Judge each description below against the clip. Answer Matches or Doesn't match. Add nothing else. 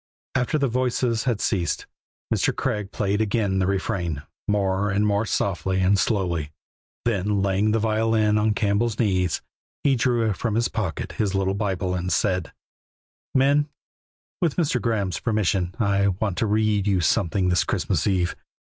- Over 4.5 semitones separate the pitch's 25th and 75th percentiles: Doesn't match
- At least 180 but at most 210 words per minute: Doesn't match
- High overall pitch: Doesn't match